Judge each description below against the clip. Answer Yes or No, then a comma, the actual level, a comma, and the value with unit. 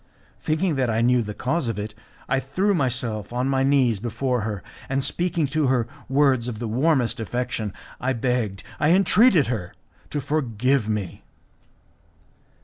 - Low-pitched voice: Yes, low, 125 Hz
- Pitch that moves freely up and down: No, average, 3.8 semitones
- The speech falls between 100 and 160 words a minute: Yes, average, 155 wpm